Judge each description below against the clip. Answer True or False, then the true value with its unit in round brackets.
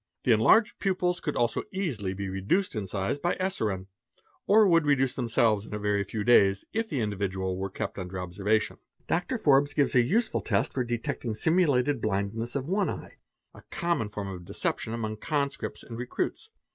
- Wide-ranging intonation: True (7.1 semitones)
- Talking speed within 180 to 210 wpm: True (185 wpm)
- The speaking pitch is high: False (115 Hz)